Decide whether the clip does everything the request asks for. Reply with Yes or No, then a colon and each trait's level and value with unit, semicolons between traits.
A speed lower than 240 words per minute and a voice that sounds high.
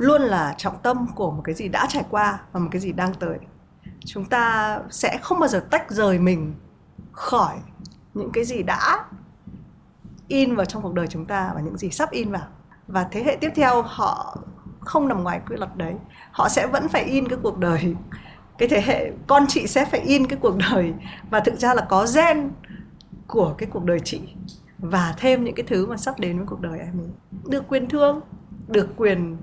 Yes: average, 210 wpm; high, 200 Hz